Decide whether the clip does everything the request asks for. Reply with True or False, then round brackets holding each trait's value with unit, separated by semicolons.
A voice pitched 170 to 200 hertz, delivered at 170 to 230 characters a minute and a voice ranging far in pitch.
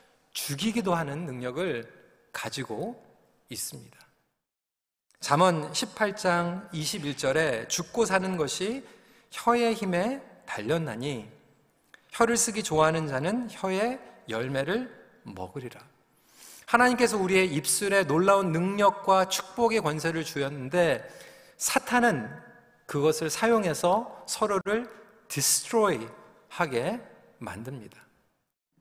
True (190 Hz; 220 characters per minute; 6.4 semitones)